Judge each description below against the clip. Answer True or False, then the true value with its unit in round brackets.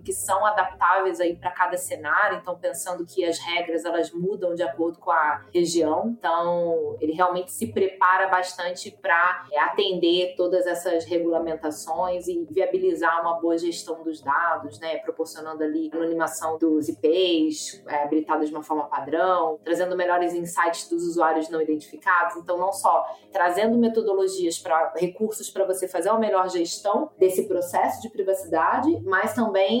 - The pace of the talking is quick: False (155 wpm)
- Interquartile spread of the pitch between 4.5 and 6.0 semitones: False (2.5 semitones)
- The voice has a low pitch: False (175 Hz)